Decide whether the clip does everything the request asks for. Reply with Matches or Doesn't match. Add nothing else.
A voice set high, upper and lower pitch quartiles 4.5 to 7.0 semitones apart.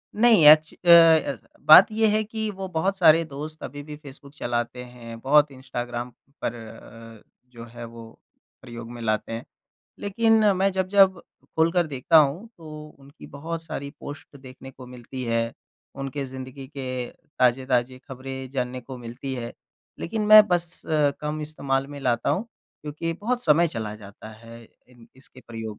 Doesn't match